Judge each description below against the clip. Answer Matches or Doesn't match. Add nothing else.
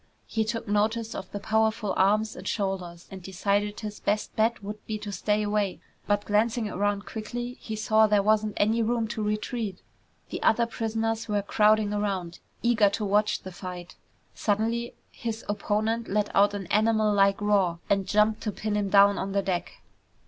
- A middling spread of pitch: Doesn't match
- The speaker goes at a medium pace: Matches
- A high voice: Matches